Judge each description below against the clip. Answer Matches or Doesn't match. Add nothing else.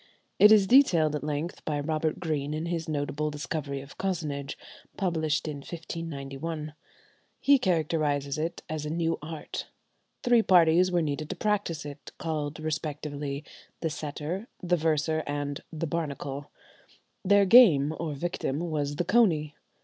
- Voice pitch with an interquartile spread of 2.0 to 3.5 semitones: Matches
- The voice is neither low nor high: Matches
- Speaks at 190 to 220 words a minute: Doesn't match